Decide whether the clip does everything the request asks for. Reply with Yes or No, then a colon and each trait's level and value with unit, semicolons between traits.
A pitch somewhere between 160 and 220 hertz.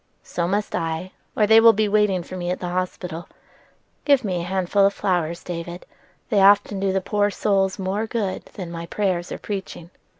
Yes: high, 190 Hz